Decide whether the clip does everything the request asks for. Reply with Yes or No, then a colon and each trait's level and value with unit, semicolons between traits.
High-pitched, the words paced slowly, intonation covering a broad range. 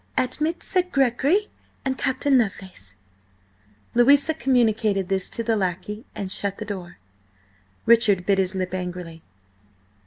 Yes: high, 215 Hz; slow, 125 wpm; wide, 5.7 semitones